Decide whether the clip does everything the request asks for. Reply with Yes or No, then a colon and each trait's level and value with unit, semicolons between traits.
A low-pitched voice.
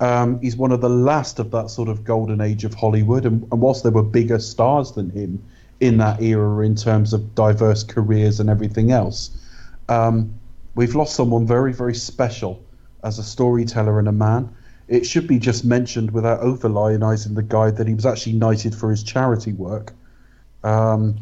Yes: low, 115 Hz